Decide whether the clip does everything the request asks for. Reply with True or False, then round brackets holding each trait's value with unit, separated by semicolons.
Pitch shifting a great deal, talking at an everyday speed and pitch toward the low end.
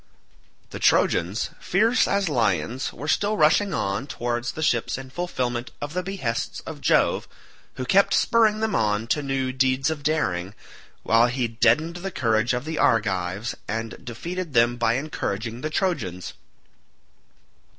True (5.8 semitones; 150 wpm; 130 Hz)